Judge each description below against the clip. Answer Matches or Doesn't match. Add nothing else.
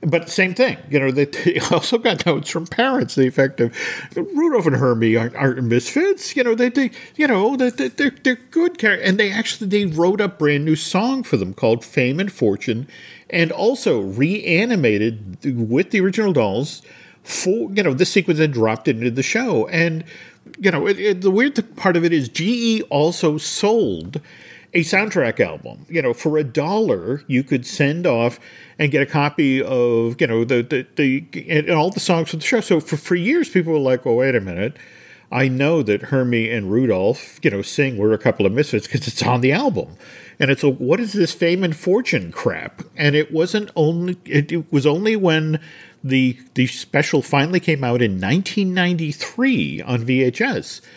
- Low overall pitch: Doesn't match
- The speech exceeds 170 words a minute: Matches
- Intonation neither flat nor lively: Doesn't match